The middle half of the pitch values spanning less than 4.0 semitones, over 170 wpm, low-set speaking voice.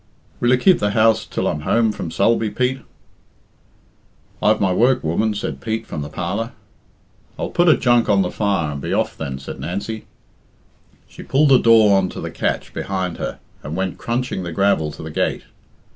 No: average, 4.8 semitones; average, 190 wpm; low, 105 Hz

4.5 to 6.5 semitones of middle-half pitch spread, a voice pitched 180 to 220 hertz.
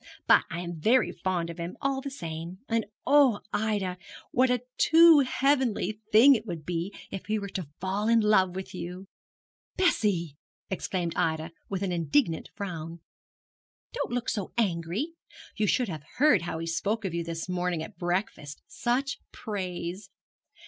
Yes: average, 5.1 semitones; high, 190 Hz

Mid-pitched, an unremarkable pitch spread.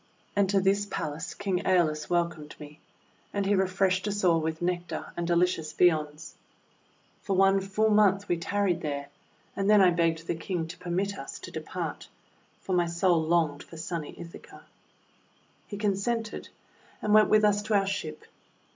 Yes: medium, 180 Hz; average, 3.3 semitones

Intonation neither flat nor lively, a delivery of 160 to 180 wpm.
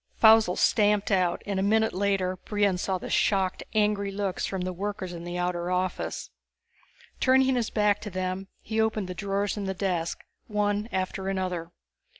No: narrow, 2.1 semitones; average, 170 wpm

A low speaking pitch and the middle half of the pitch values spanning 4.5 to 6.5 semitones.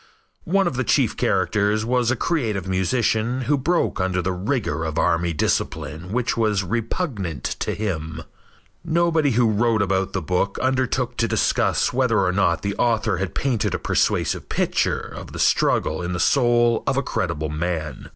Yes: low, 105 Hz; wide, 5.6 semitones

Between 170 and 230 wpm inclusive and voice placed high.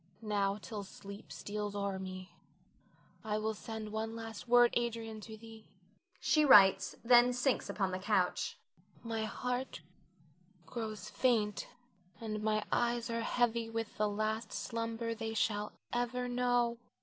No: slow, 135 wpm; high, 225 Hz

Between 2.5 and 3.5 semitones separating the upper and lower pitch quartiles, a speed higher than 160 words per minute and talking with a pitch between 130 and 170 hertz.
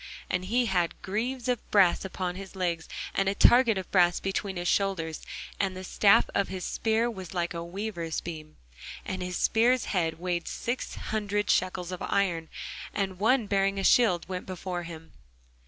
No: average, 2.8 semitones; average, 175 wpm; high, 190 Hz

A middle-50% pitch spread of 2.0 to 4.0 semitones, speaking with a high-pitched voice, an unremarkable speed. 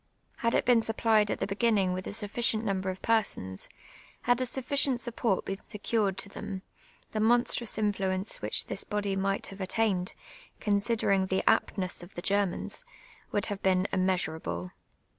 Yes: average, 3.1 semitones; high, 200 Hz; average, 165 wpm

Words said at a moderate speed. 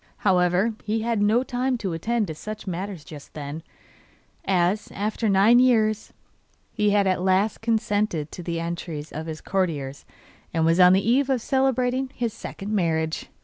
Yes: average, 165 wpm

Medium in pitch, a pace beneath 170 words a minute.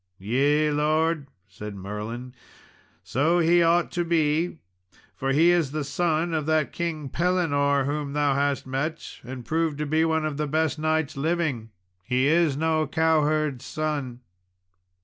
Yes: medium, 150 Hz; average, 150 wpm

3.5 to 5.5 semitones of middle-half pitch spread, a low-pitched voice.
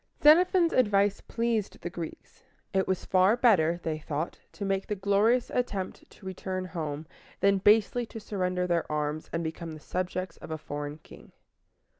No: average, 4.2 semitones; medium, 185 Hz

